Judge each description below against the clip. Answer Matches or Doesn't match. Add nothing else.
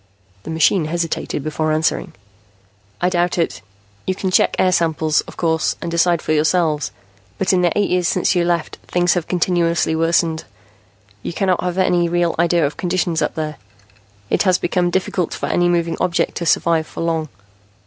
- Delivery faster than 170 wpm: Matches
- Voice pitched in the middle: Matches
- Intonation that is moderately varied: Doesn't match